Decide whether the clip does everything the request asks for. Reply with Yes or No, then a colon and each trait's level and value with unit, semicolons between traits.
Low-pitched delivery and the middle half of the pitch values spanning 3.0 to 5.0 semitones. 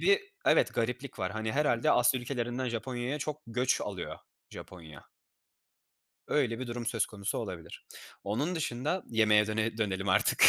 Yes: low, 120 Hz; average, 3.4 semitones